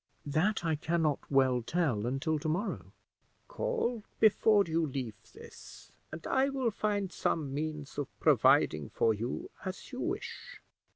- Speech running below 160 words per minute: Yes, average, 150 wpm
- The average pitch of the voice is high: No, medium, 160 Hz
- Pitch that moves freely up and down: Yes, wide, 7.1 semitones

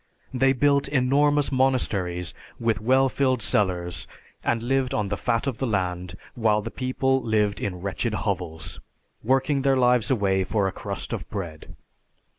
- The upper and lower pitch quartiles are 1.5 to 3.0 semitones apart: No, wide, 5.5 semitones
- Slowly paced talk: No, average, 155 wpm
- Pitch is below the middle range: Yes, low, 115 Hz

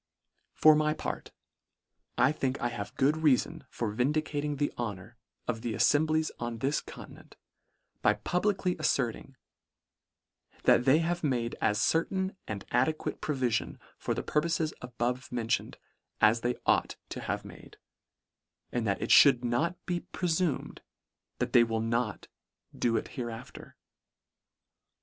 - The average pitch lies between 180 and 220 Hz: No, low, 130 Hz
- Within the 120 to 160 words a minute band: Yes, average, 145 wpm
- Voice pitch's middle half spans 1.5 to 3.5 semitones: No, average, 4.8 semitones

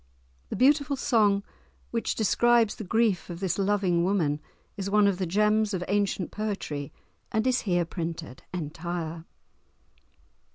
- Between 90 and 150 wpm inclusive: Yes, slow, 135 wpm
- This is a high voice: Yes, high, 200 Hz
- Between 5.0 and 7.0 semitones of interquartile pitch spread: No, average, 3.9 semitones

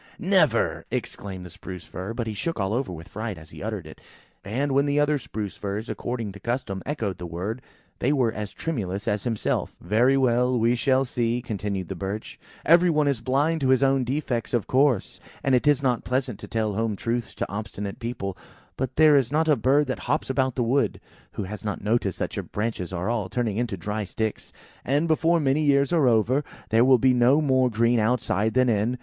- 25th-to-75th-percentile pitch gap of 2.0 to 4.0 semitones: No, average, 4.5 semitones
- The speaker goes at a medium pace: No, fast, 215 wpm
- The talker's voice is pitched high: No, low, 120 Hz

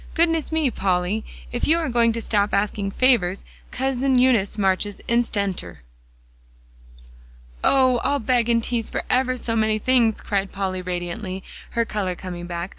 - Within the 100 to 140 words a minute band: No, average, 150 wpm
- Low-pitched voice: No, high, 220 Hz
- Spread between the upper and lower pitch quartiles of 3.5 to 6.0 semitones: Yes, average, 4.7 semitones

